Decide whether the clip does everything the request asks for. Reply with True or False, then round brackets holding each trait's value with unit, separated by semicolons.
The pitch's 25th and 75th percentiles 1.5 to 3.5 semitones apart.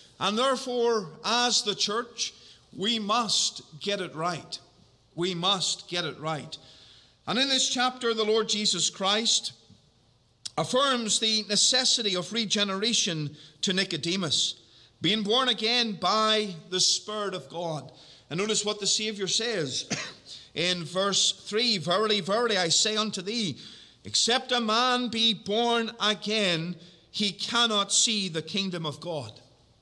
False (4.8 semitones)